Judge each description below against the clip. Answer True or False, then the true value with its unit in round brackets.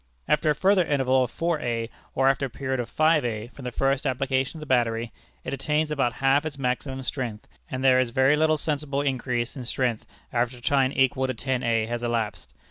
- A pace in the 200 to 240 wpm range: True (205 wpm)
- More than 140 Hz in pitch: False (130 Hz)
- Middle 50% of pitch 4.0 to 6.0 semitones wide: False (2.7 semitones)